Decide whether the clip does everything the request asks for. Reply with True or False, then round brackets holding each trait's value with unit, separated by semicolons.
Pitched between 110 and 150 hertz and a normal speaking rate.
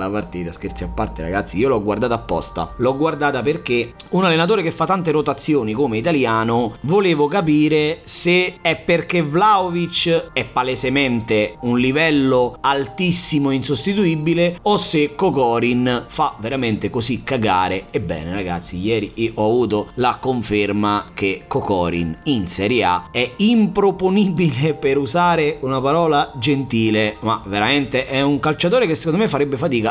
True (135 Hz; 140 wpm)